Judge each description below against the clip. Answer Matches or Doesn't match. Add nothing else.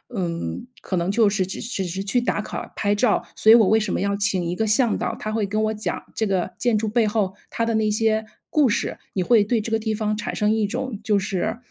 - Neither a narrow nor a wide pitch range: Doesn't match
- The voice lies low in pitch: Doesn't match